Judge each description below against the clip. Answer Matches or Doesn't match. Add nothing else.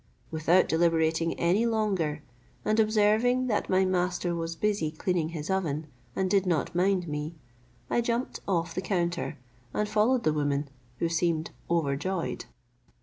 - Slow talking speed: Doesn't match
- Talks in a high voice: Doesn't match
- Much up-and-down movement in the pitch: Doesn't match